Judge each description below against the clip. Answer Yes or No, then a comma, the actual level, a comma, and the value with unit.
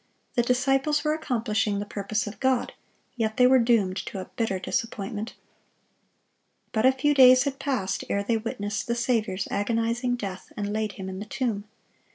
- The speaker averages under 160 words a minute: No, average, 175 wpm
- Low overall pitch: No, high, 225 Hz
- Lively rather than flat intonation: No, average, 3.7 semitones